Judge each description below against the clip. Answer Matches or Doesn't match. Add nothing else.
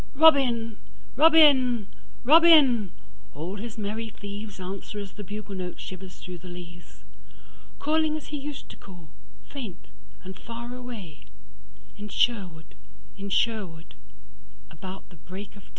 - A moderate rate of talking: Doesn't match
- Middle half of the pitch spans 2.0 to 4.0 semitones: Doesn't match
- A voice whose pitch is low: Doesn't match